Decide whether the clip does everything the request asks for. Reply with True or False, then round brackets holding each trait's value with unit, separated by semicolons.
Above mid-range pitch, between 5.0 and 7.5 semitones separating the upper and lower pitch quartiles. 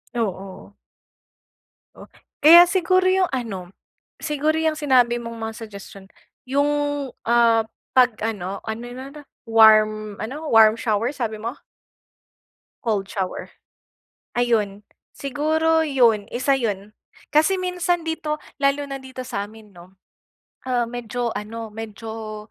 True (235 Hz; 5.3 semitones)